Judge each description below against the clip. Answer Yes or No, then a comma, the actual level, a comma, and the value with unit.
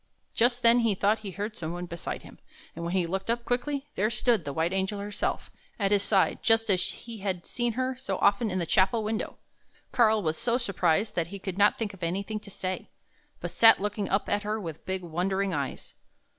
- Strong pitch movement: No, average, 3.4 semitones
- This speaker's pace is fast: Yes, fast, 220 wpm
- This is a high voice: Yes, high, 200 Hz